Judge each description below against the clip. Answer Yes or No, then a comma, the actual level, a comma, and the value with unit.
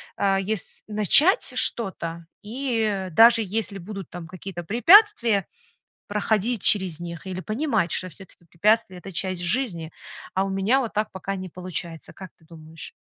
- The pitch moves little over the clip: No, average, 3.8 semitones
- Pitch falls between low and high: No, high, 195 Hz